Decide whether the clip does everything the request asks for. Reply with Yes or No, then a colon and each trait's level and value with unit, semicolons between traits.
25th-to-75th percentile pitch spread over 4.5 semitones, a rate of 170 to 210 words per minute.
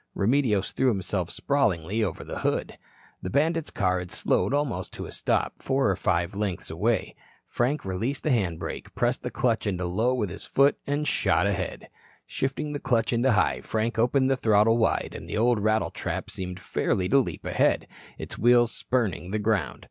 Yes: average, 5.3 semitones; average, 185 wpm